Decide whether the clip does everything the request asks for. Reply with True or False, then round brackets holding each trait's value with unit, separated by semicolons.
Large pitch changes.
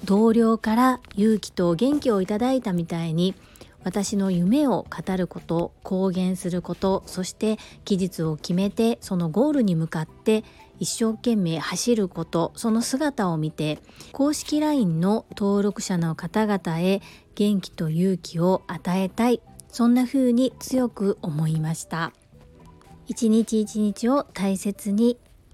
False (4.3 semitones)